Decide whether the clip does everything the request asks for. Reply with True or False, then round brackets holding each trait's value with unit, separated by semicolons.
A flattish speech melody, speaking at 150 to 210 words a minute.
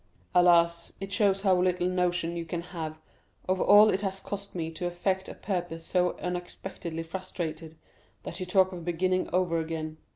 True (1.9 semitones; 170 wpm)